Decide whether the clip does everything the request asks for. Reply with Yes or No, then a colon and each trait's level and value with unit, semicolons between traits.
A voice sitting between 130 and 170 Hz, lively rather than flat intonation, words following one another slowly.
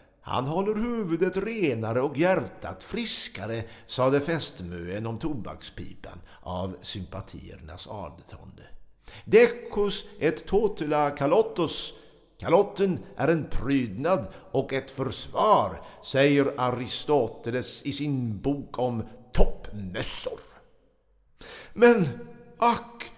Yes: low, 135 Hz; wide, 9.0 semitones; slow, 90 wpm